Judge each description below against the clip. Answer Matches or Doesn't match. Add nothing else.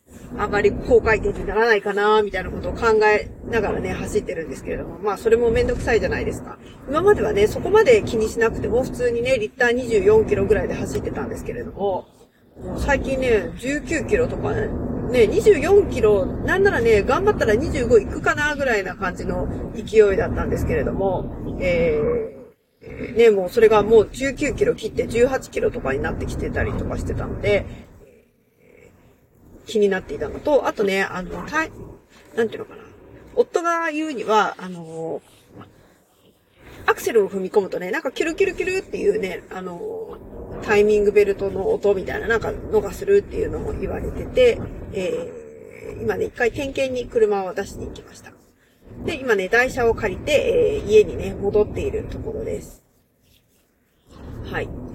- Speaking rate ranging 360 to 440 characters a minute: Doesn't match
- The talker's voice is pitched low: Doesn't match